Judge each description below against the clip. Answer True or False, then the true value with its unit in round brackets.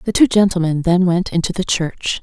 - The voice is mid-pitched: True (180 Hz)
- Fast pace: True (215 wpm)